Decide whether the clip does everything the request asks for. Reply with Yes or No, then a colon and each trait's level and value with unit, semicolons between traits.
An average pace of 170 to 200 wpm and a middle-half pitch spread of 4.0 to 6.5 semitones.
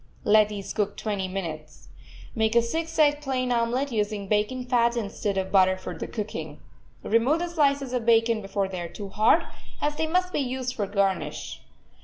Yes: average, 190 wpm; average, 4.7 semitones